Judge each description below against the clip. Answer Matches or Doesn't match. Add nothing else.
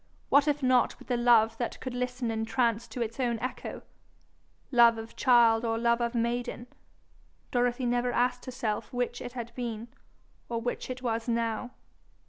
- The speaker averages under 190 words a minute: Matches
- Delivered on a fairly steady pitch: Matches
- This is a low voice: Doesn't match